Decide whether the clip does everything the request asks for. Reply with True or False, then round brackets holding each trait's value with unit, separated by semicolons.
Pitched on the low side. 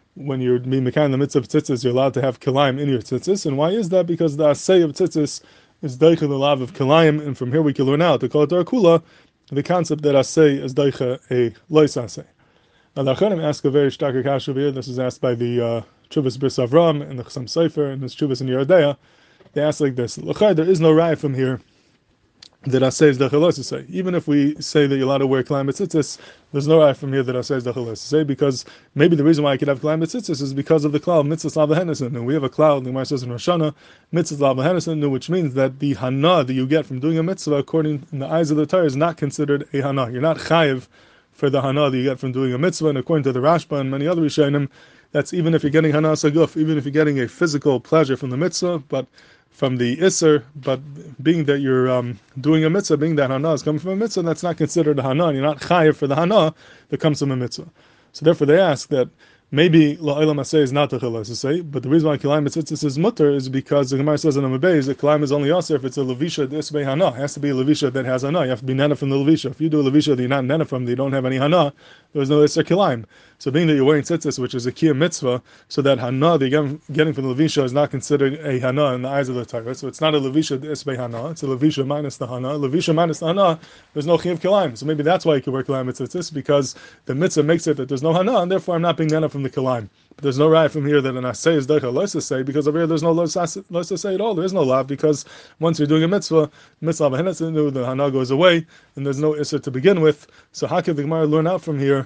False (145 Hz)